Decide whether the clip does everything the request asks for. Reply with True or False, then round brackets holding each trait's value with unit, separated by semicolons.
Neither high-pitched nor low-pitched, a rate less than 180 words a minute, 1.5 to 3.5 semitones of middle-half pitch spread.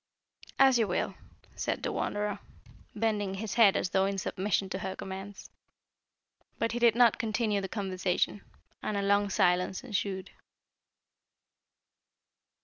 False (200 Hz; 135 wpm; 2.5 semitones)